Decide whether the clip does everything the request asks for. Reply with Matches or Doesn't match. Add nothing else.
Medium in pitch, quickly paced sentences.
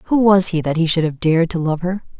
Matches